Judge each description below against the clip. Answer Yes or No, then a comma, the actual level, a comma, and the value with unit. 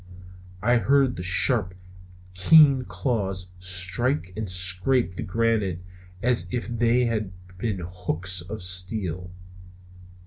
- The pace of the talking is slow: Yes, slow, 115 wpm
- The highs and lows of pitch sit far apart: No, average, 4.7 semitones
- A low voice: Yes, very low, 95 Hz